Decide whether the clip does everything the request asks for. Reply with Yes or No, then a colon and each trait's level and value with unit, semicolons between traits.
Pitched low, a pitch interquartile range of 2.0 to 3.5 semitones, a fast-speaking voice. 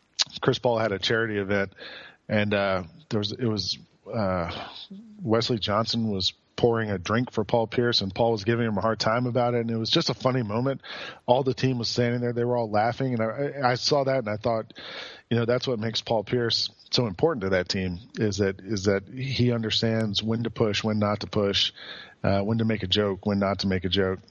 Yes: low, 110 Hz; average, 2.9 semitones; fast, 230 wpm